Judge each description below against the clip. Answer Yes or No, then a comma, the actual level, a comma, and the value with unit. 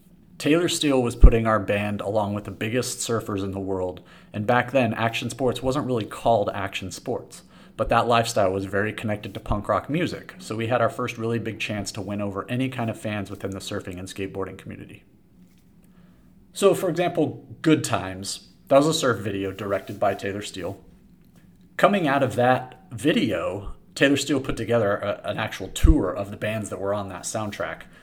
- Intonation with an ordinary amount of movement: Yes, average, 4.0 semitones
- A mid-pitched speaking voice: No, low, 110 Hz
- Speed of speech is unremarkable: Yes, average, 195 wpm